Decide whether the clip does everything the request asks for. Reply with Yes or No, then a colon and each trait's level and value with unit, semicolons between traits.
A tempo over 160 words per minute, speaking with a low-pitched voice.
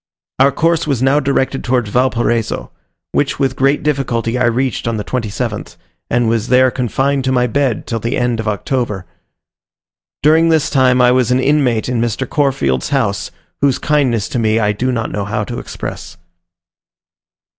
Yes: average, 170 wpm; low, 125 Hz